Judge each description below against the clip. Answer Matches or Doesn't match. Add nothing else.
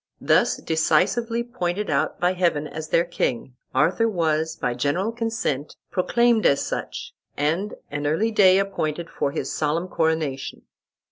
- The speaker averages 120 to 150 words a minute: Matches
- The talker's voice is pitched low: Doesn't match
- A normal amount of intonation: Matches